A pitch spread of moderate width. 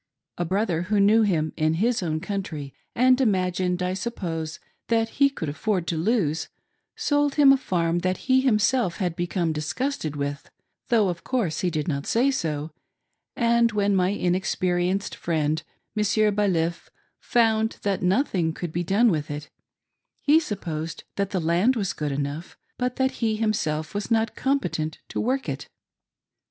No: wide, 5.7 semitones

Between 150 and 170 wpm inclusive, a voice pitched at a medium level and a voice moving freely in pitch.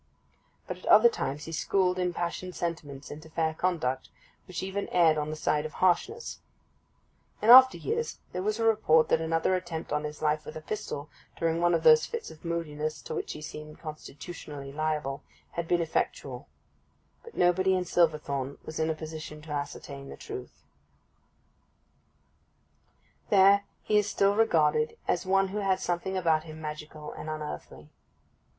No: average, 165 wpm; medium, 165 Hz; average, 3.7 semitones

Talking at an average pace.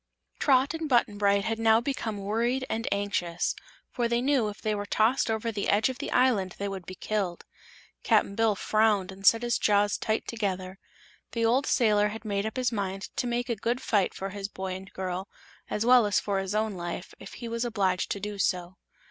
No: fast, 215 wpm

